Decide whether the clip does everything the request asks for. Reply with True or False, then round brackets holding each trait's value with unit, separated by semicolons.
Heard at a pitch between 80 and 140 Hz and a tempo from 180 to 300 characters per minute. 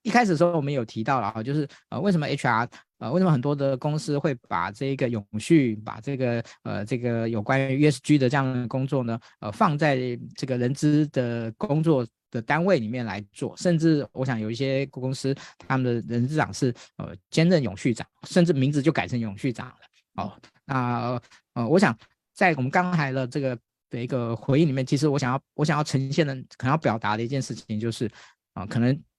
False (135 Hz; 310 characters per minute)